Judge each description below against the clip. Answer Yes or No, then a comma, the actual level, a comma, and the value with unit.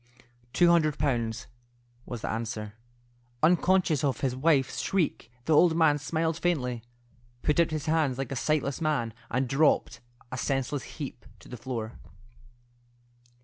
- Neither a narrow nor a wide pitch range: Yes, average, 4.3 semitones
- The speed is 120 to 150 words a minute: Yes, average, 145 wpm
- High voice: No, medium, 140 Hz